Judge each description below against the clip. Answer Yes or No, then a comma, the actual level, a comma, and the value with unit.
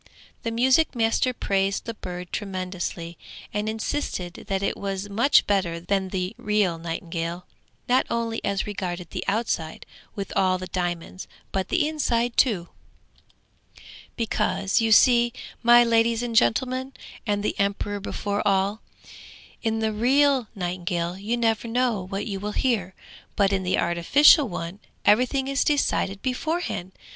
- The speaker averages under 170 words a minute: Yes, average, 140 wpm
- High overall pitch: Yes, high, 205 Hz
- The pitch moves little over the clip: No, average, 4.3 semitones